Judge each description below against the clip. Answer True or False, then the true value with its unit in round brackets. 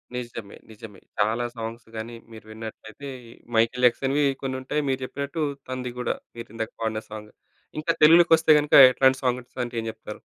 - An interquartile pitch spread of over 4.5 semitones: False (3.3 semitones)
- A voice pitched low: True (120 Hz)